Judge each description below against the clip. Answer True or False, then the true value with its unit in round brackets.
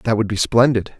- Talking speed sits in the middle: False (240 wpm)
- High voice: False (110 Hz)